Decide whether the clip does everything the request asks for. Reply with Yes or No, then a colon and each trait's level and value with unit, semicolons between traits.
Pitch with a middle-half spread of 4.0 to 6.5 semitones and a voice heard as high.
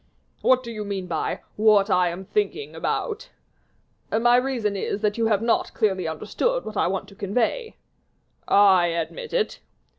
Yes: average, 4.6 semitones; high, 210 Hz